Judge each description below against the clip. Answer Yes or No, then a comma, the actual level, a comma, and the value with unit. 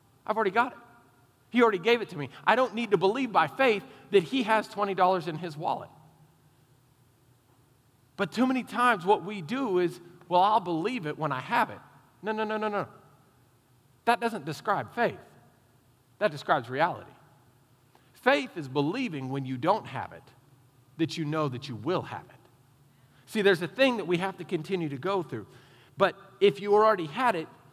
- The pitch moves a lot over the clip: Yes, wide, 7.9 semitones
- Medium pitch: Yes, medium, 160 Hz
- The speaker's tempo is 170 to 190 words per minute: Yes, average, 185 wpm